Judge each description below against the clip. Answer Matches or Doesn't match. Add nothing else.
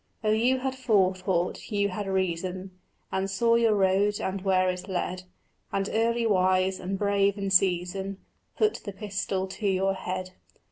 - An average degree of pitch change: Doesn't match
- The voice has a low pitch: Doesn't match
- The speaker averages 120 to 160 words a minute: Matches